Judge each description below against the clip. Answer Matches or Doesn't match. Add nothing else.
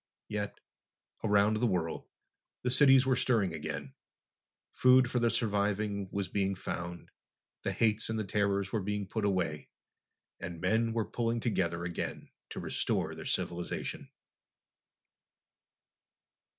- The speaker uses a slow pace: Matches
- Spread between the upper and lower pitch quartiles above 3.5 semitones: Doesn't match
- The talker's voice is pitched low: Matches